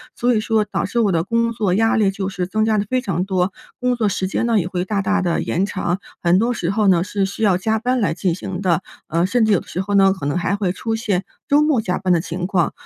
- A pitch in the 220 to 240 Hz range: No, high, 195 Hz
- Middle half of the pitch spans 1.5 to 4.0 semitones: Yes, average, 3.5 semitones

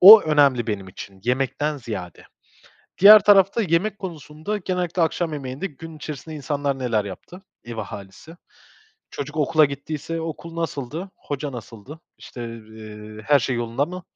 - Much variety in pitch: Yes, wide, 5.8 semitones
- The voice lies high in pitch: No, medium, 145 Hz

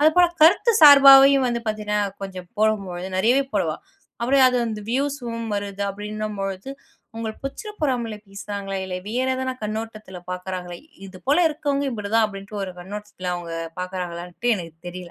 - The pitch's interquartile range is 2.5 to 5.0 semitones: No, wide, 5.5 semitones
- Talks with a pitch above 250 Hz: No, high, 215 Hz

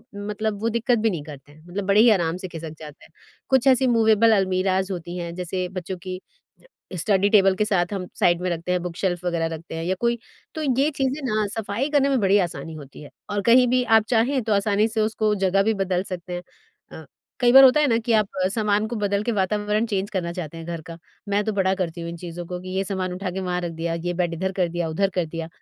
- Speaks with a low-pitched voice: No, high, 190 Hz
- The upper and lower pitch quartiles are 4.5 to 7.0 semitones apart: No, average, 3.8 semitones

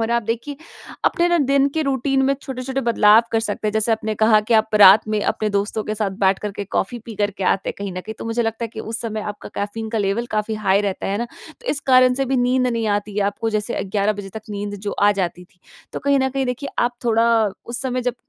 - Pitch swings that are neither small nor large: Yes, average, 3.3 semitones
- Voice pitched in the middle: No, high, 220 Hz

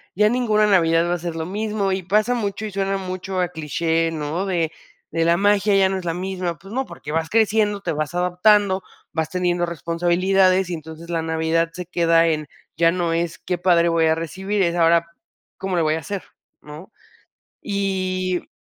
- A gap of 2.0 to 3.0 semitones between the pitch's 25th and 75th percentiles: Yes, average, 2.7 semitones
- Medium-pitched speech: Yes, medium, 180 Hz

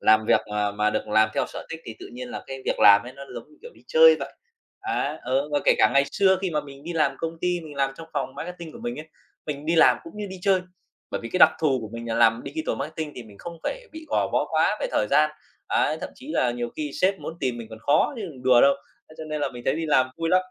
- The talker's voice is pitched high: No, medium, 150 Hz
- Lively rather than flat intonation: Yes, wide, 5.8 semitones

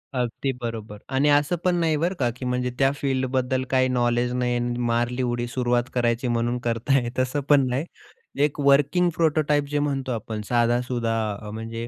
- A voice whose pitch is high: No, low, 125 Hz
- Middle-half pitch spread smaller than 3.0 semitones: Yes, narrow, 2.6 semitones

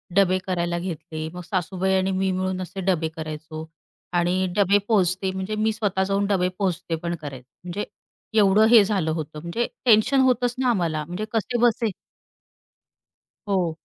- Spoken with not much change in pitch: No, average, 3.2 semitones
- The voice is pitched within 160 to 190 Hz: Yes, medium, 185 Hz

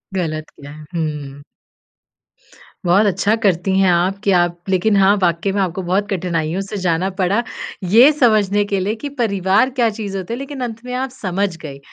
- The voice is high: Yes, high, 195 Hz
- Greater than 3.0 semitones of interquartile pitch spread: Yes, average, 3.7 semitones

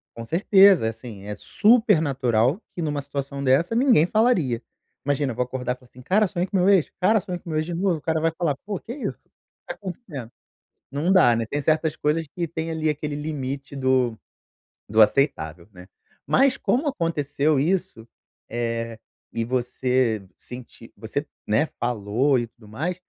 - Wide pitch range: Yes, wide, 6.1 semitones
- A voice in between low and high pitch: Yes, medium, 145 Hz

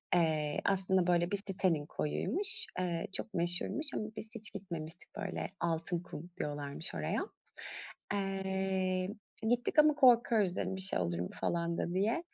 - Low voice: No, medium, 185 Hz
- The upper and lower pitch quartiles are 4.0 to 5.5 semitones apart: No, average, 3.2 semitones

